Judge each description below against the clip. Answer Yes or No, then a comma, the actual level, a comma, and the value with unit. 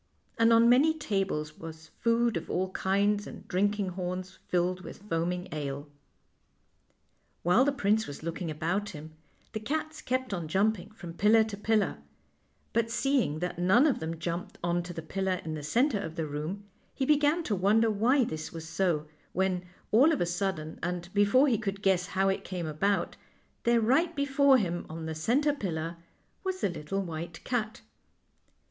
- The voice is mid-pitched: No, high, 195 Hz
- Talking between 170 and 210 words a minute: Yes, average, 180 wpm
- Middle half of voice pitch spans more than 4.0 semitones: Yes, average, 5.3 semitones